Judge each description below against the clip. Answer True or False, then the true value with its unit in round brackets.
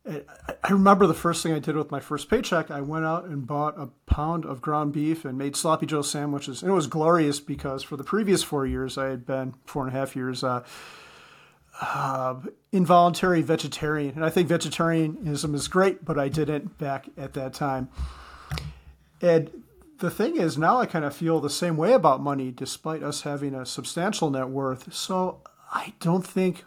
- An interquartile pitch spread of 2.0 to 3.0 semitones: False (3.7 semitones)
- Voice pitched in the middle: True (150 Hz)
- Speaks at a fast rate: False (195 wpm)